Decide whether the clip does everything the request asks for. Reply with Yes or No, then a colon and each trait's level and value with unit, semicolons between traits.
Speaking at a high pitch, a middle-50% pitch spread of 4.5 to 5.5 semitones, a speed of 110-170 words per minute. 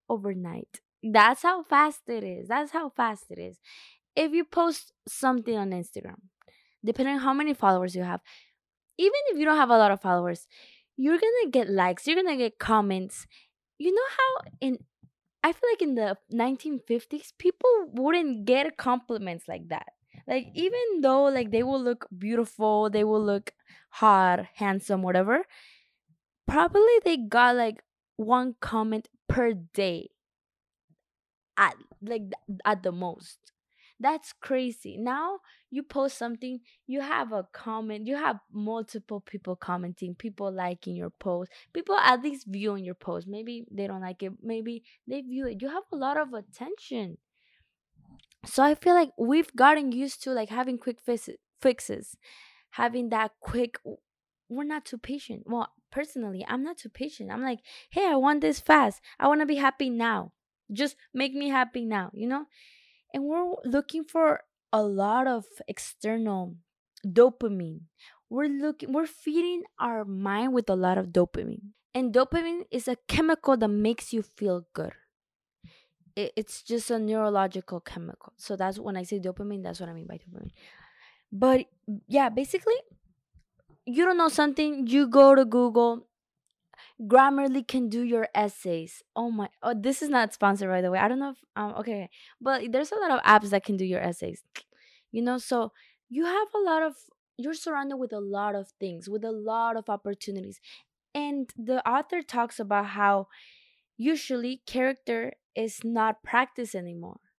Yes: high, 235 Hz; average, 5.2 semitones; average, 165 wpm